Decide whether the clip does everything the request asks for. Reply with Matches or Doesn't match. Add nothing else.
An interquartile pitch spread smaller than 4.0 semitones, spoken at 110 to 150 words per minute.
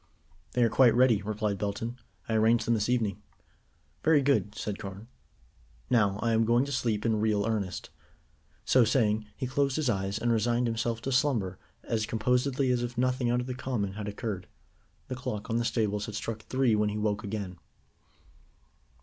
Doesn't match